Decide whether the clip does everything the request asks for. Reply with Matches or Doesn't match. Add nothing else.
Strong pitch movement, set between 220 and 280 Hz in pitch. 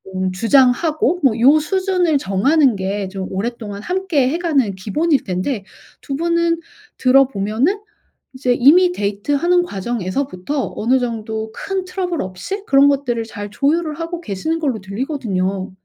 Matches